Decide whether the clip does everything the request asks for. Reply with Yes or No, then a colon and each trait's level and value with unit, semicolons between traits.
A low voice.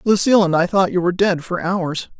No: medium, 185 Hz